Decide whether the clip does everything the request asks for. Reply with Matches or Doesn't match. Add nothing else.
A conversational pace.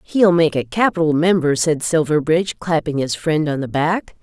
Matches